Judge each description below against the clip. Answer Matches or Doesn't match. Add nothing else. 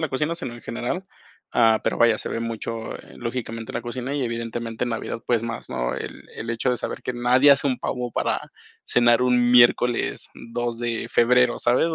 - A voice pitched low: Matches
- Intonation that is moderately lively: Doesn't match